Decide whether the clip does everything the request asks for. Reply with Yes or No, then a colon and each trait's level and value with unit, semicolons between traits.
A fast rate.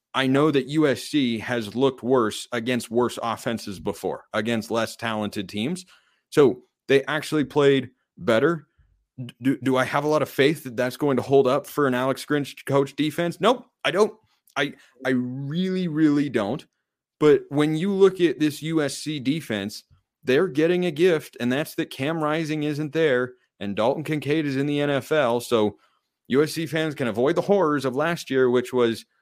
No: average, 175 wpm